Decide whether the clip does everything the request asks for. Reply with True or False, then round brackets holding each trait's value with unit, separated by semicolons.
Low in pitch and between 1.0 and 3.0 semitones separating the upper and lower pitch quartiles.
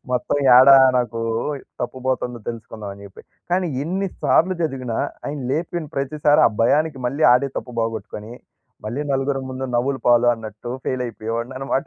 False (130 Hz; 3.6 semitones)